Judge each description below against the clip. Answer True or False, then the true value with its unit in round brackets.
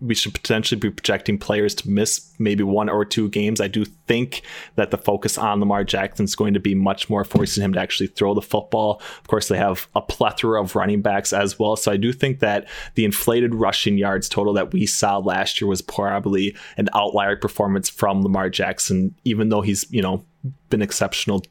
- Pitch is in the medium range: False (105 Hz)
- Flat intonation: True (1.8 semitones)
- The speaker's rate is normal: False (210 wpm)